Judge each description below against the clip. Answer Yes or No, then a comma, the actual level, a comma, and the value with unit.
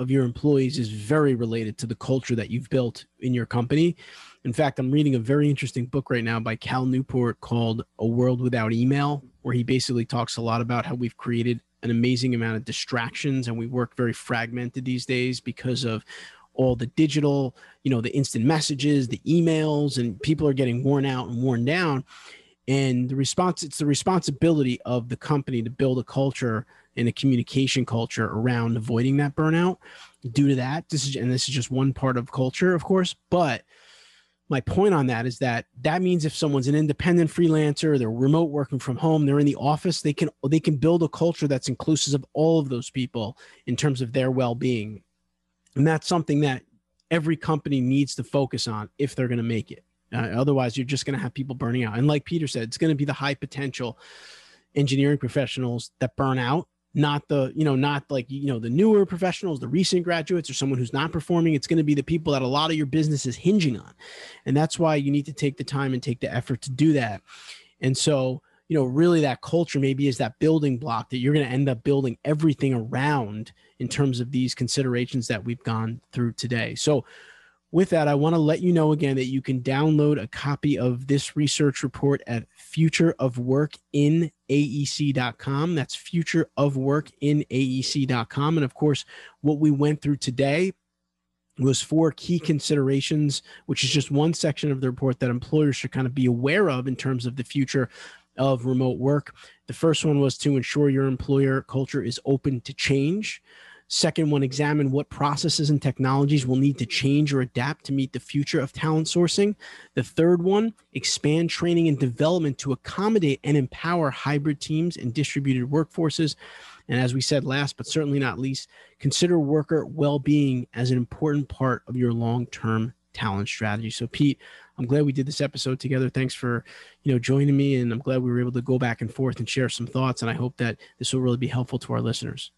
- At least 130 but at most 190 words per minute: No, fast, 205 wpm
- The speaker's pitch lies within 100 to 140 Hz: Yes, low, 135 Hz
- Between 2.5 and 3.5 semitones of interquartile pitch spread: Yes, average, 3.1 semitones